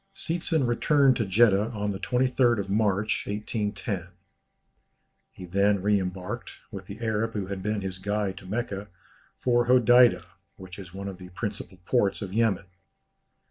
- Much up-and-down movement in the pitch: No, average, 3.3 semitones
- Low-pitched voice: Yes, low, 105 Hz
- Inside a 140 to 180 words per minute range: Yes, average, 150 wpm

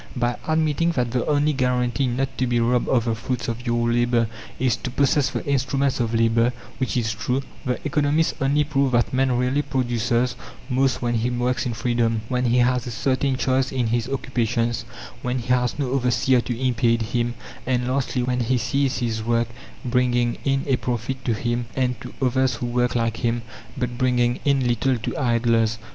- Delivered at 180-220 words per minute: Yes, average, 190 wpm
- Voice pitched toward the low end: Yes, low, 125 Hz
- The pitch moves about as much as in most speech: No, narrow, 1.8 semitones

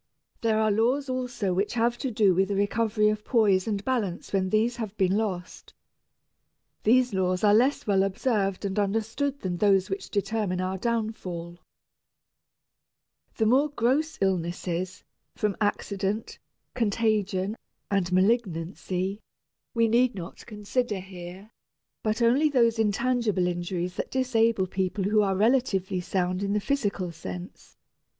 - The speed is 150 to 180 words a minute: No, slow, 135 wpm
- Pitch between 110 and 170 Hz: No, high, 205 Hz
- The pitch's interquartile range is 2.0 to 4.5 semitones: Yes, average, 3.6 semitones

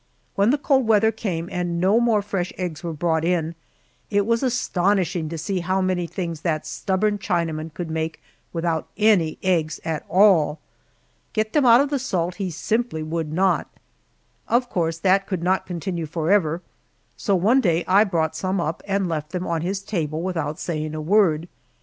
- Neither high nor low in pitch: Yes, medium, 180 Hz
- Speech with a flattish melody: No, average, 3.6 semitones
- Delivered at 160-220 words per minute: Yes, average, 180 wpm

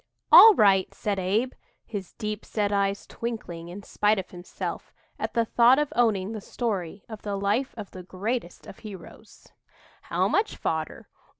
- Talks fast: No, average, 165 wpm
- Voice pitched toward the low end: No, high, 205 Hz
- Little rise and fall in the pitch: No, average, 3.2 semitones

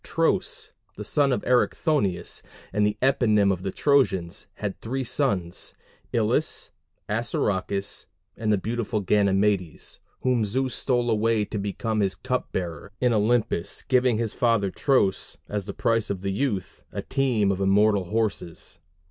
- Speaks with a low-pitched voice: Yes, low, 105 Hz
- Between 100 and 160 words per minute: Yes, average, 150 wpm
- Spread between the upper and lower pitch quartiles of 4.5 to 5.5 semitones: No, average, 3.7 semitones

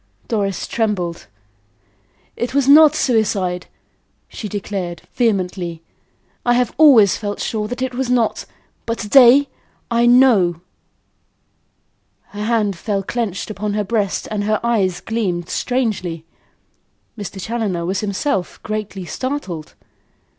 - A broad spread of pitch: No, average, 4.0 semitones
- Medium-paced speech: No, slow, 120 wpm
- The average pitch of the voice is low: No, high, 210 Hz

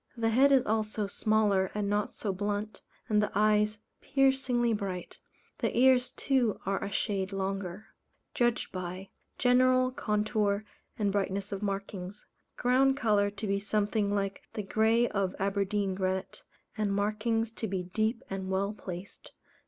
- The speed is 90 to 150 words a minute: Yes, average, 145 wpm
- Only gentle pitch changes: Yes, narrow, 2.3 semitones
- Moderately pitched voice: No, high, 210 Hz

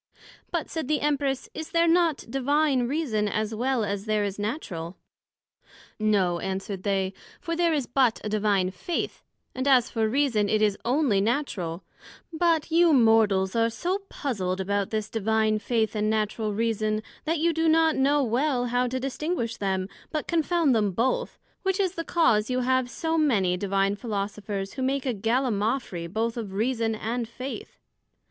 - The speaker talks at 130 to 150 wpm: No, average, 165 wpm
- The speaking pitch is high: Yes, high, 230 Hz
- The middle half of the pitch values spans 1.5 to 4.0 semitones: No, wide, 5.5 semitones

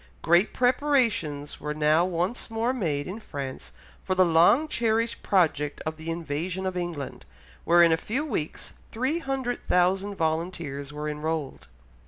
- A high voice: No, medium, 175 Hz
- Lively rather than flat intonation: Yes, wide, 6.4 semitones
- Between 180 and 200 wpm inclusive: No, average, 140 wpm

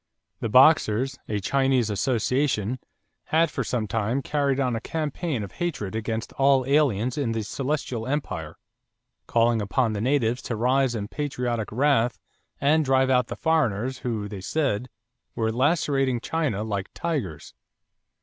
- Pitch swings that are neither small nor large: Yes, average, 3.9 semitones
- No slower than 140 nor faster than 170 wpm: Yes, average, 145 wpm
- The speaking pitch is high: No, low, 125 Hz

